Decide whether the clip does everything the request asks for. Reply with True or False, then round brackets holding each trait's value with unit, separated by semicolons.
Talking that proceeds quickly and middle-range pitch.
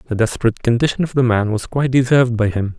False (235 wpm; 120 Hz)